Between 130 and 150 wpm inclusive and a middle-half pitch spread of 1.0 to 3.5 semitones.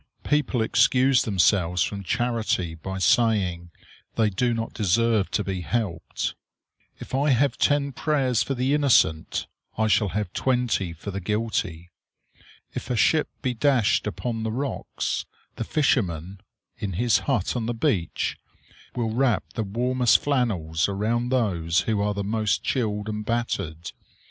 No: average, 145 wpm; average, 4.4 semitones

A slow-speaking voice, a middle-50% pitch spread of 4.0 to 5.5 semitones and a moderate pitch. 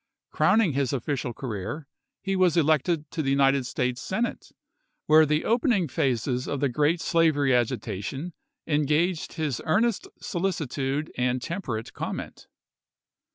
Yes: slow, 125 wpm; average, 4.4 semitones; medium, 150 Hz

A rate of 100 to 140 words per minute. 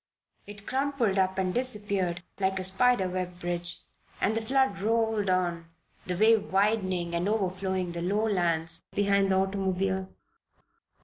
Yes: slow, 135 wpm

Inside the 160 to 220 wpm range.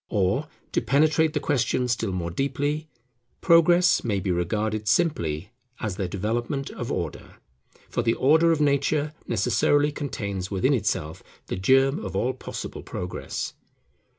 No: average, 140 wpm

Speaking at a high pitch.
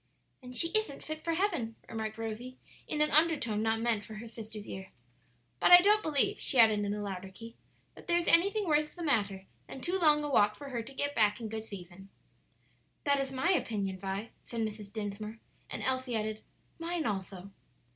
Yes: high, 230 Hz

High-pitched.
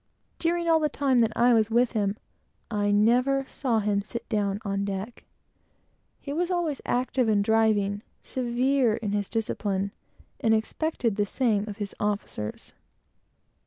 Yes: high, 225 Hz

